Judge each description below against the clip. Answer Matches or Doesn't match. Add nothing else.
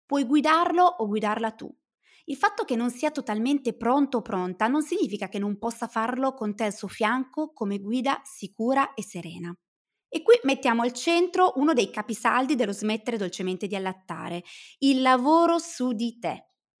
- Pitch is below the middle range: Doesn't match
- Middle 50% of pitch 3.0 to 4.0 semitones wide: Doesn't match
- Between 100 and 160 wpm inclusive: Doesn't match